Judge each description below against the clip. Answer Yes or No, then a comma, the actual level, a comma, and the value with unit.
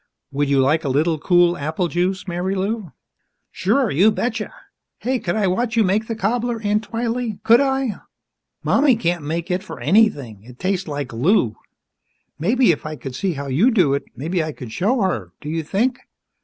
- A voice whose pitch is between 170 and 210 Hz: Yes, medium, 185 Hz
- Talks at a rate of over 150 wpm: Yes, average, 185 wpm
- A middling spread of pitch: No, wide, 6.8 semitones